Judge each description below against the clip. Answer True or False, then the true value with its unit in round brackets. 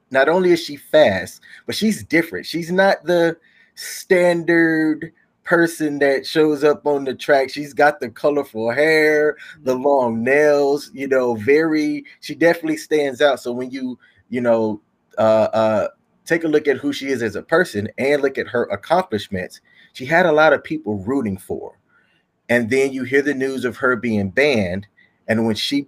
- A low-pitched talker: False (145 Hz)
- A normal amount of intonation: True (4.2 semitones)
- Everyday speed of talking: True (180 wpm)